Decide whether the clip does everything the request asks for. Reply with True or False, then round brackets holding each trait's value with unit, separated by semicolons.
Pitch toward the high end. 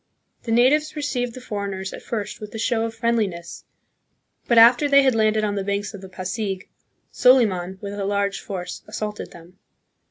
True (210 Hz)